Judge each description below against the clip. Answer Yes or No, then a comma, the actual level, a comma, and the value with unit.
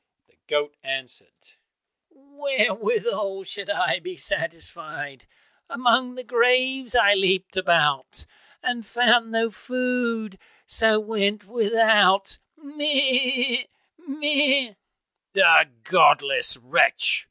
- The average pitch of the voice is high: Yes, high, 235 Hz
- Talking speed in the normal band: No, slow, 90 wpm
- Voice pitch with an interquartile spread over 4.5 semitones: Yes, average, 5.2 semitones